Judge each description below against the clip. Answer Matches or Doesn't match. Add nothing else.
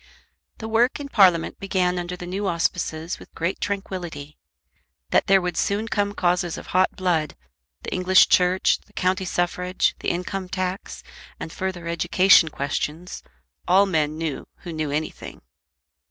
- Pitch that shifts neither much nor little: Doesn't match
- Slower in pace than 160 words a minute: Matches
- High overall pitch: Doesn't match